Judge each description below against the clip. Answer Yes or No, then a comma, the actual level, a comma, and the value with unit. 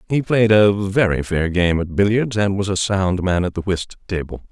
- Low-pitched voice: Yes, very low, 95 Hz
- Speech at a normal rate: No, fast, 225 wpm